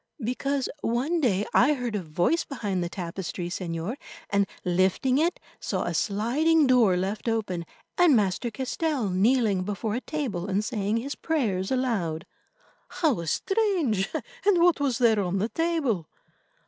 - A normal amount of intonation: No, wide, 6.6 semitones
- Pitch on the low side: No, high, 225 Hz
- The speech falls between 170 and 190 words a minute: No, average, 150 wpm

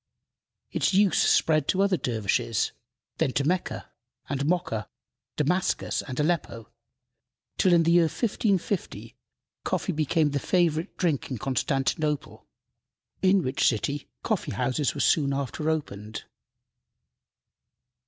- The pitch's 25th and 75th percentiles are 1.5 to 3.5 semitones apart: No, average, 4.6 semitones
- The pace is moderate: No, slow, 115 wpm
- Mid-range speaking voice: Yes, medium, 155 Hz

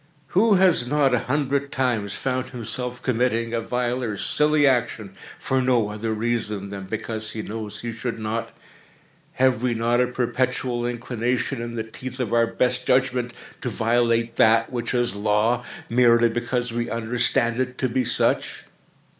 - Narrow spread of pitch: Yes, narrow, 1.9 semitones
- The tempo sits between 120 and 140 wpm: No, average, 165 wpm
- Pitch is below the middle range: Yes, low, 120 Hz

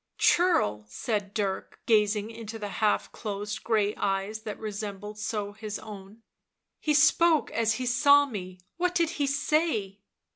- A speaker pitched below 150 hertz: No, high, 215 Hz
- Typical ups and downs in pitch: Yes, average, 3.9 semitones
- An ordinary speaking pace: Yes, average, 160 wpm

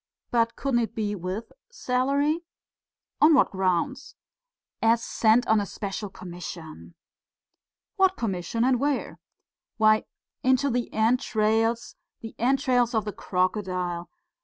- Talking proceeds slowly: Yes, slow, 115 wpm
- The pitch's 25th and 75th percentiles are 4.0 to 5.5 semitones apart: Yes, average, 4.6 semitones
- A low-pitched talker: No, high, 225 Hz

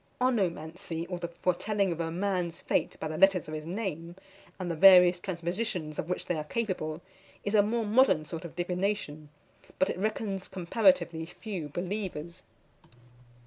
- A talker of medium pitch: Yes, medium, 180 Hz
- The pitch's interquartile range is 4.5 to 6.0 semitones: No, average, 3.2 semitones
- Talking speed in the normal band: Yes, average, 155 wpm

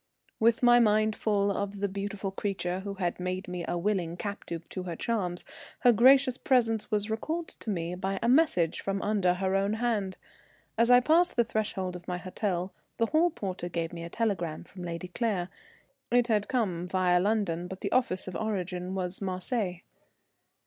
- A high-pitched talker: Yes, high, 195 Hz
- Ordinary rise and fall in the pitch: Yes, average, 3.7 semitones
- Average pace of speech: Yes, average, 185 wpm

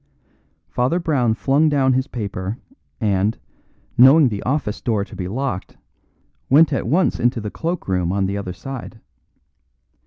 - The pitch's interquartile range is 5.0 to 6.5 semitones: Yes, wide, 5.5 semitones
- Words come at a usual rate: Yes, average, 150 wpm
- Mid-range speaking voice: No, low, 120 Hz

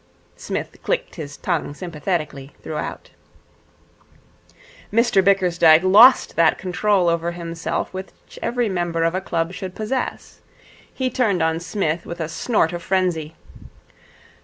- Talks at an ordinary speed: No, slow, 125 wpm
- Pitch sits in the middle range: Yes, medium, 175 Hz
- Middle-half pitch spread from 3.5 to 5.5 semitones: No, average, 3.0 semitones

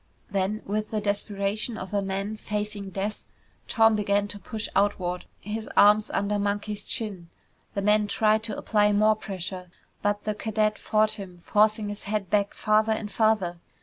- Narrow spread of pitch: Yes, narrow, 1.2 semitones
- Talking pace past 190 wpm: No, average, 165 wpm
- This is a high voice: Yes, high, 210 Hz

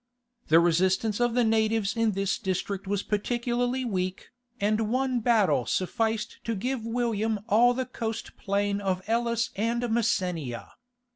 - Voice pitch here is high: Yes, high, 220 Hz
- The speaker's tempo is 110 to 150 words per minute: Yes, average, 140 wpm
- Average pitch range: Yes, average, 3.3 semitones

